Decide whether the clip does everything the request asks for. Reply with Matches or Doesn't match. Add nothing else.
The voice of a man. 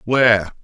Matches